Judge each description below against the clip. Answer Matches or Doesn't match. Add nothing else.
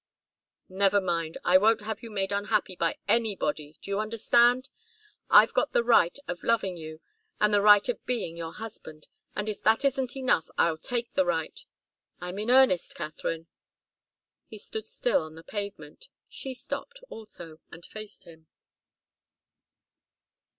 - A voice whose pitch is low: Doesn't match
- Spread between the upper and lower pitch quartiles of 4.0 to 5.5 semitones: Matches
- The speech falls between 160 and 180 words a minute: Doesn't match